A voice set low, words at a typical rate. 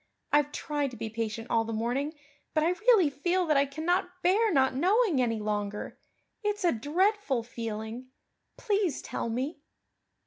No: very high, 285 Hz; average, 160 wpm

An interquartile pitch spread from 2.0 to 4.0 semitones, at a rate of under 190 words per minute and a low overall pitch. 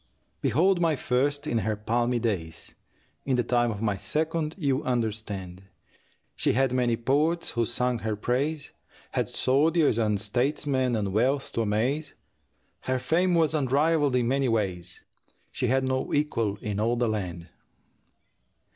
No: average, 4.7 semitones; average, 145 wpm; low, 125 Hz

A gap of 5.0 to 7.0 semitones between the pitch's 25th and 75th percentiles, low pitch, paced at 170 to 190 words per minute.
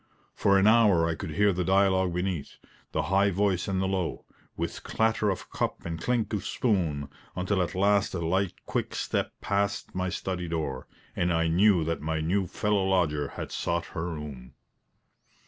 No: average, 3.2 semitones; very low, 95 Hz; average, 180 wpm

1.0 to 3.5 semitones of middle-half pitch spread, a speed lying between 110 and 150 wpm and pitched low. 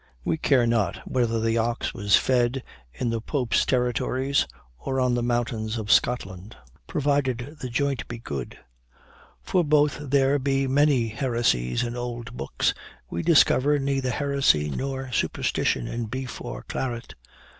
Yes: average, 3.0 semitones; average, 145 wpm; low, 125 Hz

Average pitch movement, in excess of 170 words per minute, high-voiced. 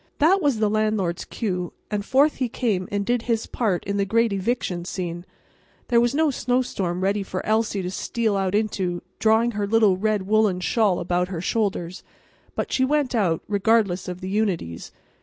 Yes: average, 3.8 semitones; average, 180 wpm; high, 205 Hz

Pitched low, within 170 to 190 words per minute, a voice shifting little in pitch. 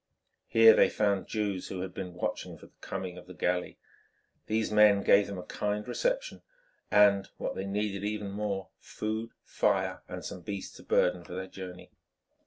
Yes: low, 100 Hz; average, 180 wpm; narrow, 2.3 semitones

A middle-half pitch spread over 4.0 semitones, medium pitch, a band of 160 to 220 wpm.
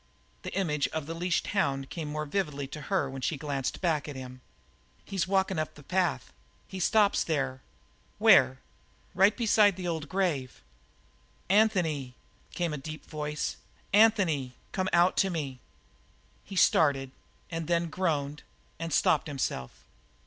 No: average, 4.8 semitones; medium, 160 Hz; average, 150 wpm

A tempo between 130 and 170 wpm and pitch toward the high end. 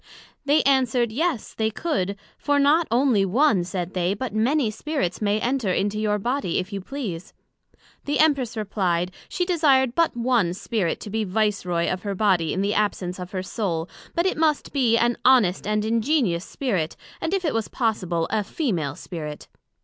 No: average, 180 wpm; high, 215 Hz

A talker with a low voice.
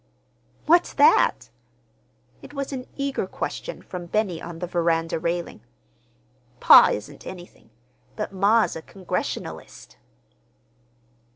No: medium, 185 Hz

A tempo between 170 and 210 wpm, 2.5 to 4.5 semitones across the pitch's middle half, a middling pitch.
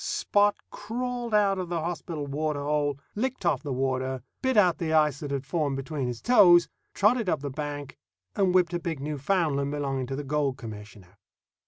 No: average, 185 wpm; average, 5.0 semitones; medium, 150 Hz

